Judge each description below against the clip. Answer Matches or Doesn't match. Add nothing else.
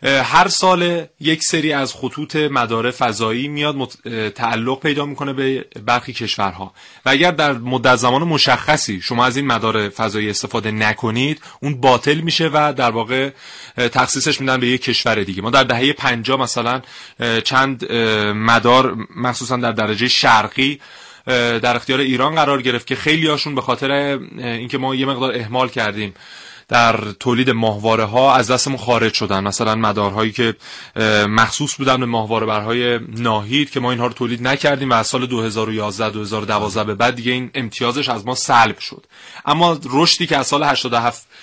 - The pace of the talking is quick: Matches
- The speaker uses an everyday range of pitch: Matches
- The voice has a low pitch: Matches